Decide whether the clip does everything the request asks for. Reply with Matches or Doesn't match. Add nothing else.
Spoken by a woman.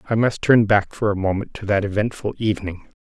Doesn't match